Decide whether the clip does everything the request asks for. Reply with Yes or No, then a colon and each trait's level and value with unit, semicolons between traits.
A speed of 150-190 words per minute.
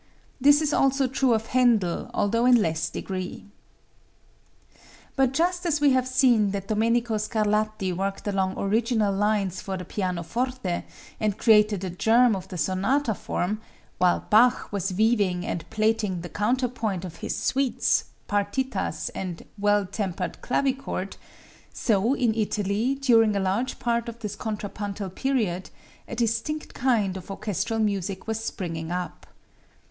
No: average, 140 wpm